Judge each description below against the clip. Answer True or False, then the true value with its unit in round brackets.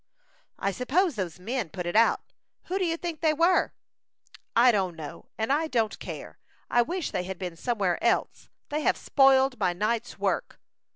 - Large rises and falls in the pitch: True (8.0 semitones)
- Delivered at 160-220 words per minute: True (180 wpm)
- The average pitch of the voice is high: True (235 Hz)